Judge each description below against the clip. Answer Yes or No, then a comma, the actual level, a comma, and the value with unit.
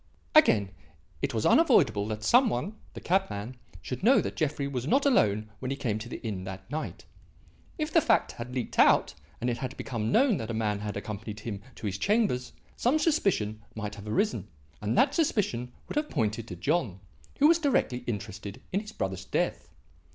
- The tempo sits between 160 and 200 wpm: Yes, average, 195 wpm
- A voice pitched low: Yes, low, 120 Hz